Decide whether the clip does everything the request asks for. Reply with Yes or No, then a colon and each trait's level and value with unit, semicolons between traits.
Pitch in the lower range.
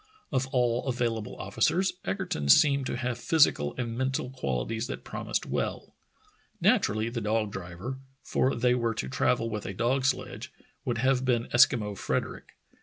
Yes: low, 120 Hz